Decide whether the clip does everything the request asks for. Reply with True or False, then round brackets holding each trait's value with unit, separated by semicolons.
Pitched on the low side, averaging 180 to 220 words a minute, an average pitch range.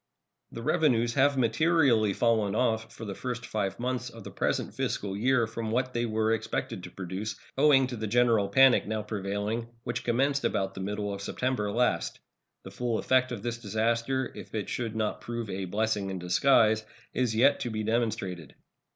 True (115 Hz; 185 wpm; 3.0 semitones)